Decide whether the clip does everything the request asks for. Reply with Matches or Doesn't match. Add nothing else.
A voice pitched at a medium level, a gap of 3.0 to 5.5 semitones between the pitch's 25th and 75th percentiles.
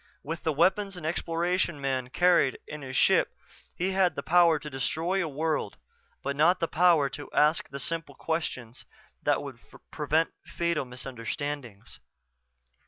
Matches